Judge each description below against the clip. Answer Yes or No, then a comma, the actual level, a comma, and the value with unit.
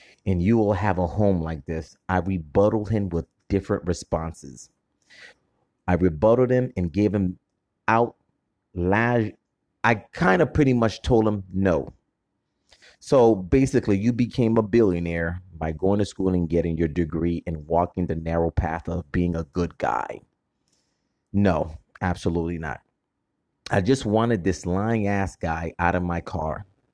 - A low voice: Yes, very low, 95 Hz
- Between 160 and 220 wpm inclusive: No, average, 150 wpm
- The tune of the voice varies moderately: Yes, average, 4.0 semitones